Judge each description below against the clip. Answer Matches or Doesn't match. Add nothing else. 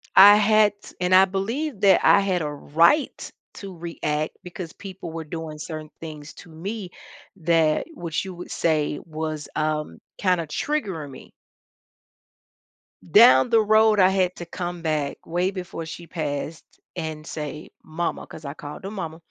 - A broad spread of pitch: Doesn't match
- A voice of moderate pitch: Matches